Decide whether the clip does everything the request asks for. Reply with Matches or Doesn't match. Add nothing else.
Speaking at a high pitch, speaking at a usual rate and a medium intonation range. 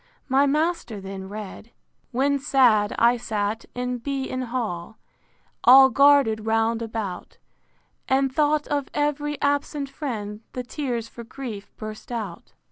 Doesn't match